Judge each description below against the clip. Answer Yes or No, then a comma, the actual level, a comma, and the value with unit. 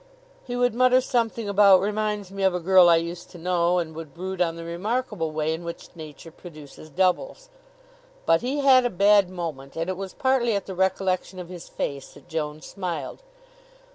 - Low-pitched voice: No, medium, 185 Hz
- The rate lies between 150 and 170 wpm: No, average, 195 wpm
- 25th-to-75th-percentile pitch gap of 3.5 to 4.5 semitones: Yes, average, 3.9 semitones